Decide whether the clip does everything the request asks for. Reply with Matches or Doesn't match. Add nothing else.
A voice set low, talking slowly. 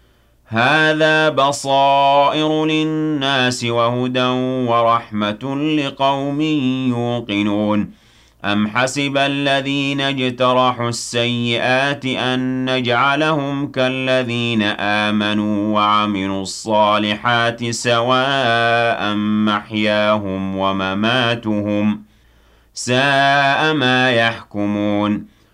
Matches